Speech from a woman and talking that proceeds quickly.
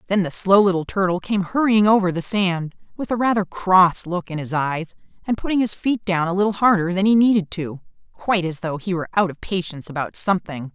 Yes: female; fast, 220 wpm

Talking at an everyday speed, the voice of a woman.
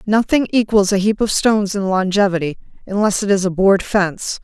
Yes: average, 190 wpm; female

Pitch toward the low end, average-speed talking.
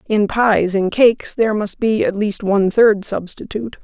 No: high, 210 Hz; average, 190 wpm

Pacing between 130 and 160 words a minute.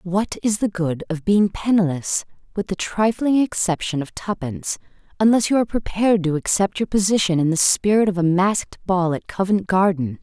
No: average, 170 wpm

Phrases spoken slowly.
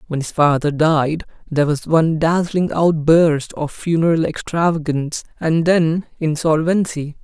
Yes: slow, 125 wpm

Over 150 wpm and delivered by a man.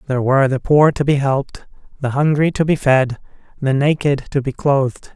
Yes: average, 200 wpm; male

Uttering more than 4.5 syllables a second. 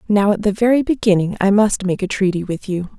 Yes: 5.7 syllables/s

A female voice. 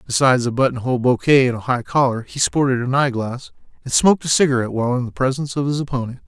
No: male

